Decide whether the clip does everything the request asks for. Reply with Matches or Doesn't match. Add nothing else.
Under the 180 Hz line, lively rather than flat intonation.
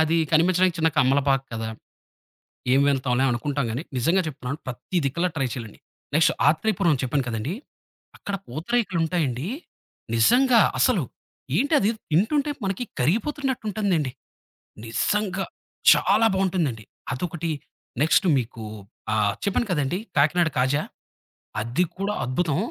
Matches